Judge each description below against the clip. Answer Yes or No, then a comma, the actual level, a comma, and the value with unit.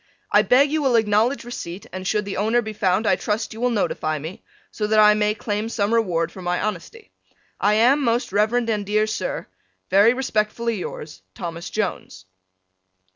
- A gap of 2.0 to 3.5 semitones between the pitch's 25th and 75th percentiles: Yes, average, 3.1 semitones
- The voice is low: No, high, 210 Hz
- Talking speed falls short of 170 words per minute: No, average, 180 wpm